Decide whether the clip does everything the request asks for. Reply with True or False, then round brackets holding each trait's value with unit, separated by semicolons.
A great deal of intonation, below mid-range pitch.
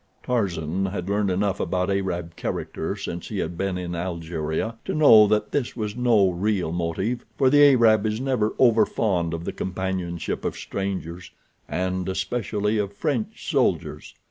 False (4.0 semitones; 95 Hz)